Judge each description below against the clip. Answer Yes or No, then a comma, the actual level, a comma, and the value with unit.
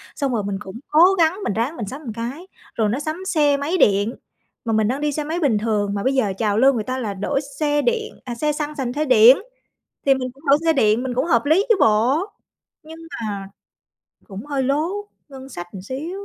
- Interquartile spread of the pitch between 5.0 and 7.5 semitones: Yes, wide, 5.5 semitones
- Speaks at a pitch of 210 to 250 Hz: No, very high, 265 Hz